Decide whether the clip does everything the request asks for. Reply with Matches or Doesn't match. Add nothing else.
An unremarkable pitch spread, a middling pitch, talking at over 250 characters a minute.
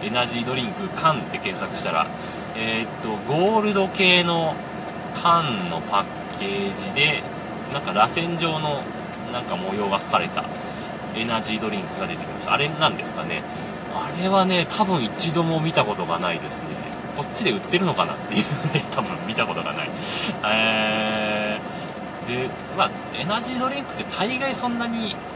Matches